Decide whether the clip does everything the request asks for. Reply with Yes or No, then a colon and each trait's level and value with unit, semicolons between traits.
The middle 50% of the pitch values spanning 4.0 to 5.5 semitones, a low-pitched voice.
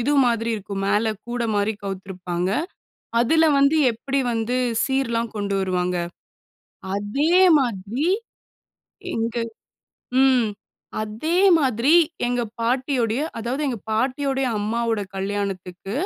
No: average, 4.4 semitones; high, 230 Hz